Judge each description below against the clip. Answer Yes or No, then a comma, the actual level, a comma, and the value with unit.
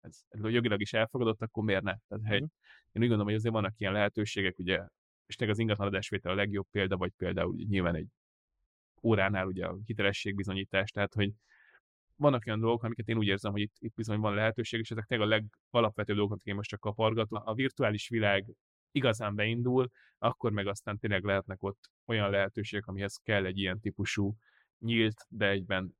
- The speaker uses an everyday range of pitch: No, narrow, 2.2 semitones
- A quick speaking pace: Yes, fast, 185 wpm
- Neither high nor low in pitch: No, low, 105 Hz